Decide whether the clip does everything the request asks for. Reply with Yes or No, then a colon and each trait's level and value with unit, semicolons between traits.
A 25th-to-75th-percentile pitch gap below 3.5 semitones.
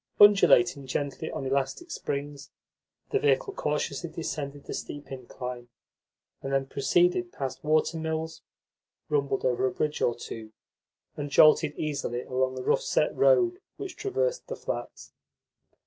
No: average, 4.2 semitones